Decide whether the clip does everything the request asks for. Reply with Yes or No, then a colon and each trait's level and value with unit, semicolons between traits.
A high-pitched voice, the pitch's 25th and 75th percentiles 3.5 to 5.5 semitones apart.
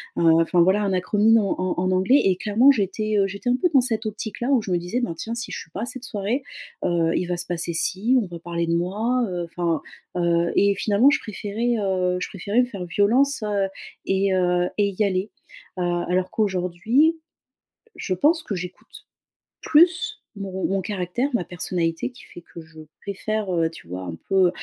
Yes: high, 195 Hz; average, 4.0 semitones